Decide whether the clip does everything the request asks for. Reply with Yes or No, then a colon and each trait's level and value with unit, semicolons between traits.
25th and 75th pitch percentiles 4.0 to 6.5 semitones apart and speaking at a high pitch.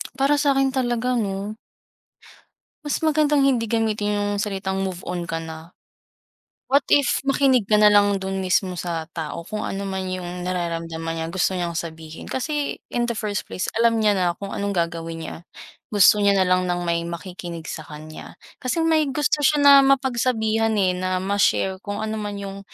Yes: average, 5.2 semitones; high, 200 Hz